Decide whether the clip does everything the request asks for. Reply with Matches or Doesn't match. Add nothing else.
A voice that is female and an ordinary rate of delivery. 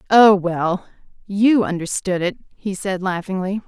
Doesn't match